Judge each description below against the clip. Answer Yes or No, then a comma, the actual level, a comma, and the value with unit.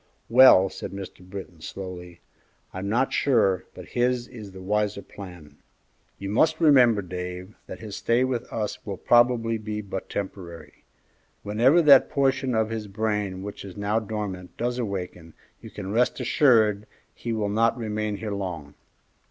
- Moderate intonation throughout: Yes, average, 3.8 semitones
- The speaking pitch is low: Yes, low, 105 Hz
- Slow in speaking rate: No, average, 155 wpm